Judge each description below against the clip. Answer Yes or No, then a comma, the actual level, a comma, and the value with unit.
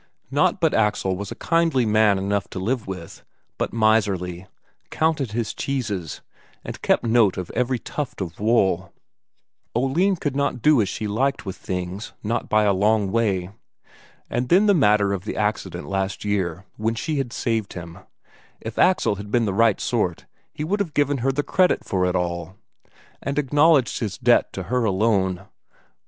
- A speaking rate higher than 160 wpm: Yes, average, 175 wpm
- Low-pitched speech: Yes, low, 110 Hz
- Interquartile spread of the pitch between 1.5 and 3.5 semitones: No, wide, 5.5 semitones